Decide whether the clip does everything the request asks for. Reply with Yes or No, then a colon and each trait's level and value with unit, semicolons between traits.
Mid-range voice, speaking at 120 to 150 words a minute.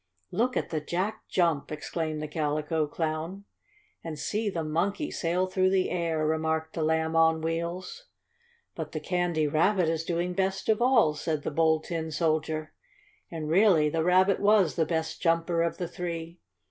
No: medium, 165 Hz; average, 165 wpm